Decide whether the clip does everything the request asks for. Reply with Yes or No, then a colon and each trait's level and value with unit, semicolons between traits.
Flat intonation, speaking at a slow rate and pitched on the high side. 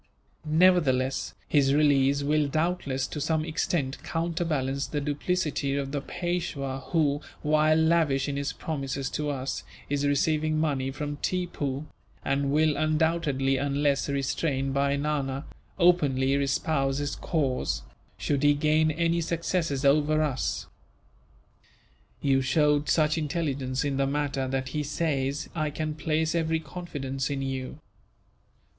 No: narrow, 2.3 semitones; slow, 130 wpm; medium, 145 Hz